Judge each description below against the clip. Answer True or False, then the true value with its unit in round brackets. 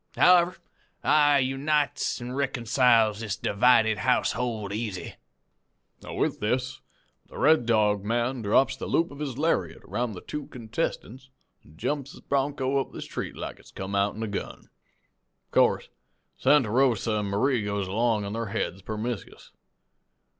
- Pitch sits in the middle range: False (120 Hz)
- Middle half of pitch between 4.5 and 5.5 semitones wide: False (4.1 semitones)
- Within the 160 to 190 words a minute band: False (145 wpm)